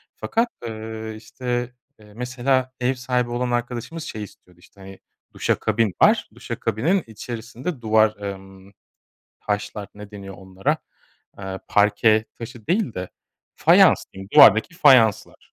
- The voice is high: No, low, 110 Hz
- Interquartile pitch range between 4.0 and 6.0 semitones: No, average, 3.3 semitones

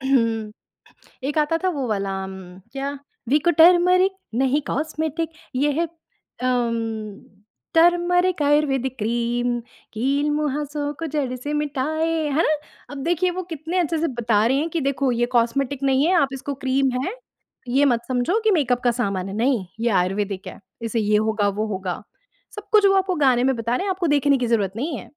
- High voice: Yes, very high, 275 Hz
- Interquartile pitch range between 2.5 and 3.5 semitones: No, average, 5.2 semitones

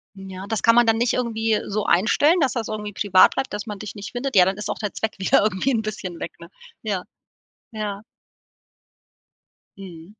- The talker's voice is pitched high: Yes, high, 210 Hz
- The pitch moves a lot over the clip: No, average, 2.8 semitones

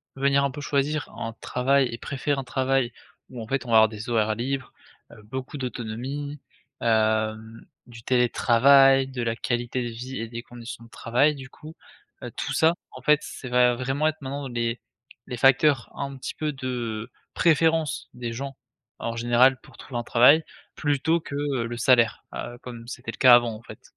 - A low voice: Yes, low, 125 Hz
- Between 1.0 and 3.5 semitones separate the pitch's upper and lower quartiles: Yes, average, 2.9 semitones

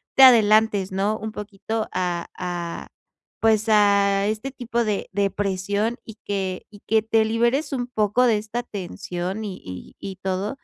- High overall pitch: Yes, high, 210 Hz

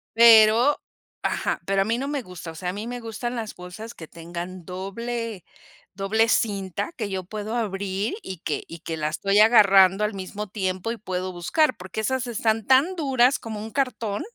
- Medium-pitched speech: No, high, 210 Hz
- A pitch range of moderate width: Yes, average, 3.7 semitones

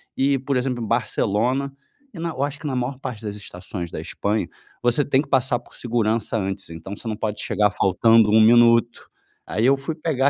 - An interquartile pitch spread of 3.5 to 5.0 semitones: Yes, average, 4.0 semitones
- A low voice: Yes, low, 120 Hz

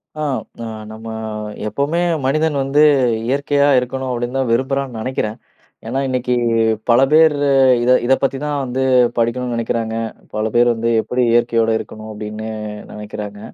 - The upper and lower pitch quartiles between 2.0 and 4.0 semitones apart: Yes, average, 3.1 semitones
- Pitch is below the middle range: Yes, low, 125 Hz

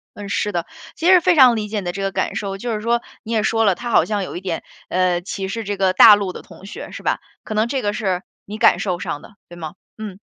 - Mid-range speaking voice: No, high, 205 Hz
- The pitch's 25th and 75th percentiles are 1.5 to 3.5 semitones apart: Yes, average, 3.0 semitones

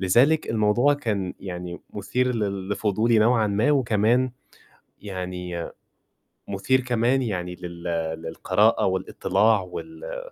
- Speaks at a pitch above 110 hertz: No, low, 105 Hz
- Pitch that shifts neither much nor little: Yes, average, 4.9 semitones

